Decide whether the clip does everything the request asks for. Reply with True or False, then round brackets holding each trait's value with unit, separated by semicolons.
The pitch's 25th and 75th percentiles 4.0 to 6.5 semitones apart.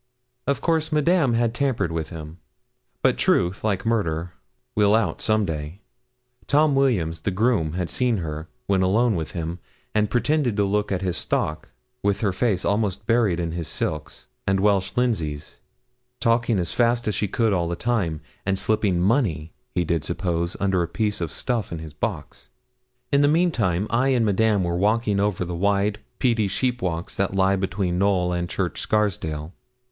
True (4.9 semitones)